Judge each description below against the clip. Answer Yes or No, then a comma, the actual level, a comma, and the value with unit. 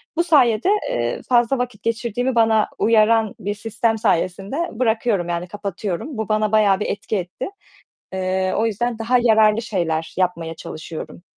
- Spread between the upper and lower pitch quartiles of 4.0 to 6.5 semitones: No, average, 3.6 semitones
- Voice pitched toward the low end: No, high, 215 Hz